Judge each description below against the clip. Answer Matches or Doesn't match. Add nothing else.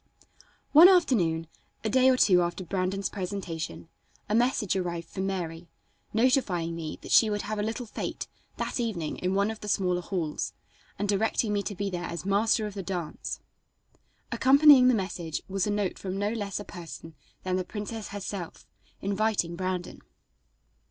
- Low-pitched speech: Doesn't match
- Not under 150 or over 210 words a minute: Matches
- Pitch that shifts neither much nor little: Matches